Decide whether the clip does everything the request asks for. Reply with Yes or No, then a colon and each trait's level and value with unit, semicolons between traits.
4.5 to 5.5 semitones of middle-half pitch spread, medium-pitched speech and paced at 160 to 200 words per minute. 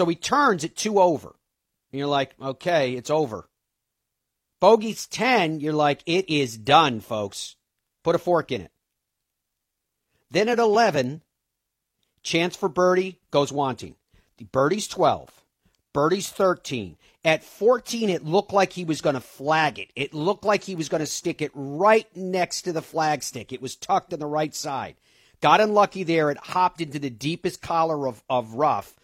Yes: average, 4.9 semitones; medium, 160 Hz; average, 165 wpm